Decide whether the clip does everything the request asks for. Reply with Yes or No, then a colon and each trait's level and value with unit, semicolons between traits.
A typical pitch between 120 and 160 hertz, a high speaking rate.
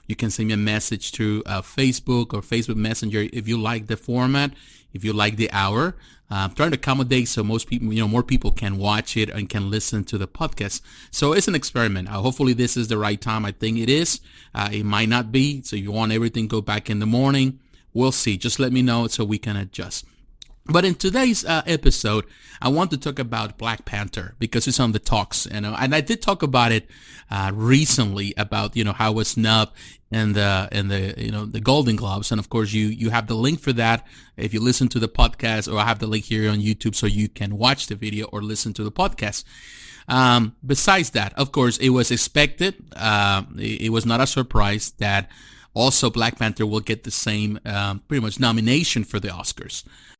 No: low, 110 Hz; fast, 225 wpm